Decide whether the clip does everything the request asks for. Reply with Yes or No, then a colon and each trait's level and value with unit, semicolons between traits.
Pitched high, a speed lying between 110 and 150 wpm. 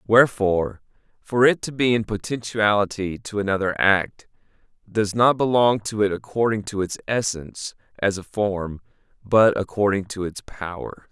No: low, 105 Hz; average, 145 wpm